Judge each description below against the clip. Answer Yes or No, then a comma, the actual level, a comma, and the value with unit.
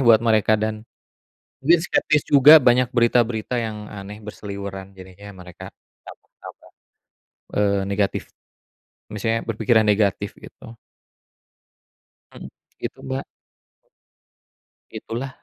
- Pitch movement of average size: Yes, average, 3.1 semitones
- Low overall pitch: Yes, low, 110 Hz